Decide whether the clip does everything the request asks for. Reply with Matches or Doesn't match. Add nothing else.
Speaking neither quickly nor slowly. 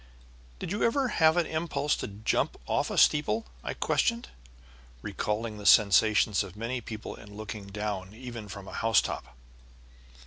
Matches